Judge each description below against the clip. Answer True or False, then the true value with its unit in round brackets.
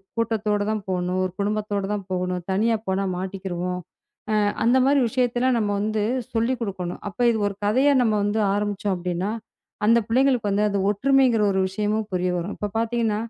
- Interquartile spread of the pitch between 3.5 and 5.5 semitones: False (3.1 semitones)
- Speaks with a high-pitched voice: True (210 Hz)